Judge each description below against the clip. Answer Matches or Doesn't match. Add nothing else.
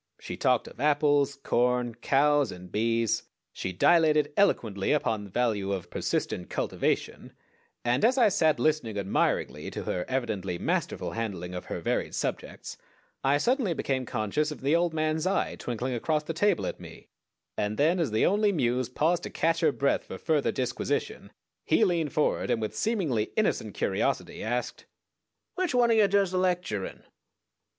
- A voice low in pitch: Doesn't match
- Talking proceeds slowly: Doesn't match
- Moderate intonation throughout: Doesn't match